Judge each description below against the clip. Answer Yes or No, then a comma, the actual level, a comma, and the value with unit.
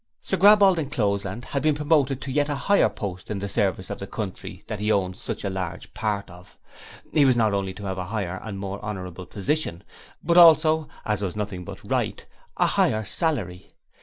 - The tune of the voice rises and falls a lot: Yes, wide, 7.2 semitones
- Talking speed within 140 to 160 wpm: No, average, 200 wpm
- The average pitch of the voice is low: Yes, low, 105 Hz